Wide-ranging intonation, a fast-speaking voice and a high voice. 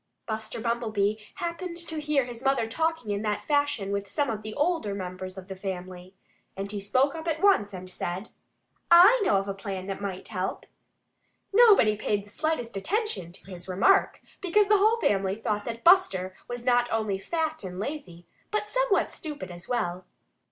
No: wide, 8.5 semitones; average, 180 wpm; high, 220 Hz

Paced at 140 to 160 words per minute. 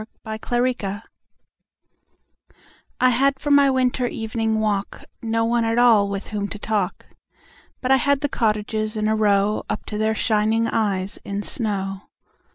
Yes: average, 155 wpm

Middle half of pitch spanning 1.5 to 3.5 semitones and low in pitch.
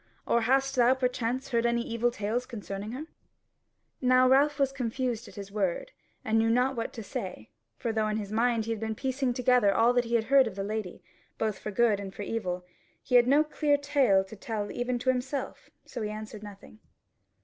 No: average, 3.2 semitones; high, 235 Hz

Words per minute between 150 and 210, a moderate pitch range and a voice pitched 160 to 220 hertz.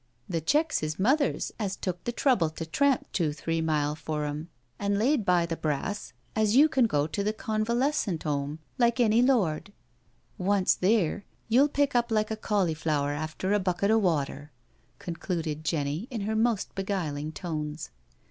No: average, 175 wpm; wide, 6.1 semitones; high, 190 Hz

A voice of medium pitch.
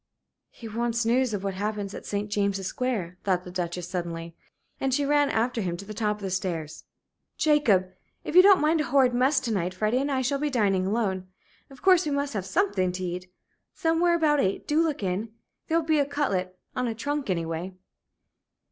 No: high, 220 Hz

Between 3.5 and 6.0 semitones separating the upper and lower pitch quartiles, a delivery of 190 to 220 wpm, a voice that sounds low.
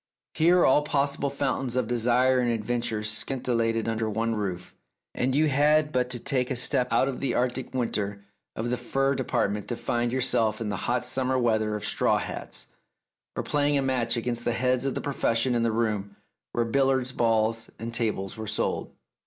No: average, 2.7 semitones; average, 195 wpm; low, 120 Hz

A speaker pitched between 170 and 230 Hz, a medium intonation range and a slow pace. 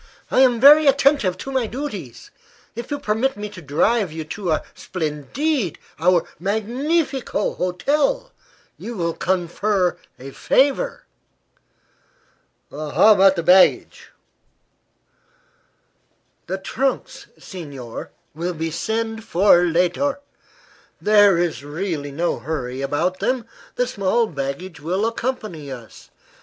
No: high, 190 Hz; wide, 6.7 semitones; slow, 115 wpm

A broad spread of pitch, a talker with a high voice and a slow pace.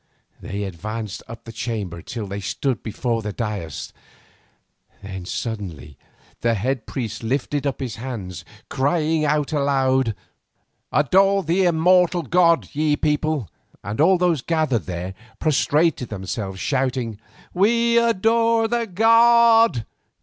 No: wide, 8.1 semitones; low, 135 Hz; slow, 120 wpm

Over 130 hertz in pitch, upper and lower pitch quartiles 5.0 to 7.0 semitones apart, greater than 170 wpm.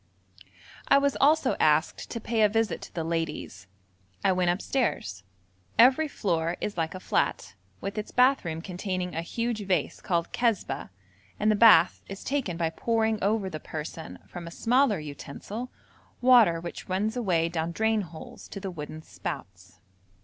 No: medium, 185 Hz; wide, 5.4 semitones; average, 165 wpm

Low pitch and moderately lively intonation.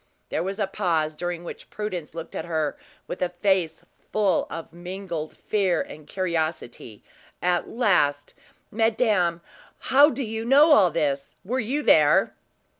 No: medium, 180 Hz; average, 4.9 semitones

